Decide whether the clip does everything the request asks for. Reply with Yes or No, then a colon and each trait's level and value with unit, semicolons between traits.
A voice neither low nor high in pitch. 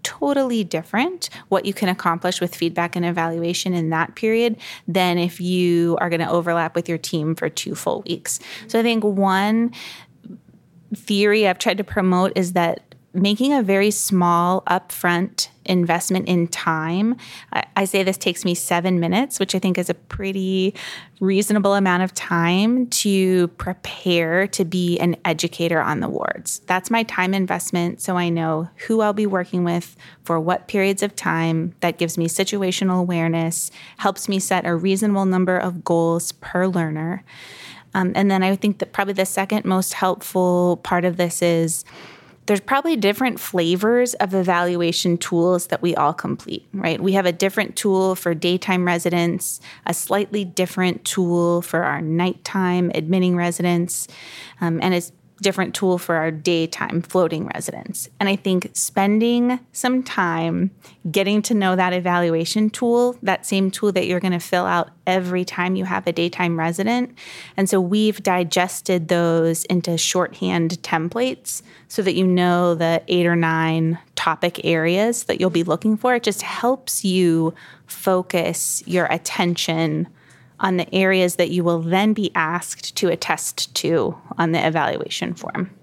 Yes: medium, 180 Hz